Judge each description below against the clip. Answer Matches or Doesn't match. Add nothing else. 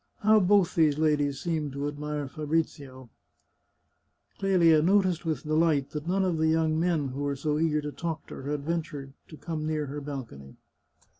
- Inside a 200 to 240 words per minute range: Doesn't match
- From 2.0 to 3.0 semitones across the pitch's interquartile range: Matches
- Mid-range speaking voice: Matches